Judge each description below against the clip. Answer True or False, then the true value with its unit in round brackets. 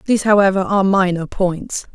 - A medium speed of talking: True (155 wpm)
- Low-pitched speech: False (195 Hz)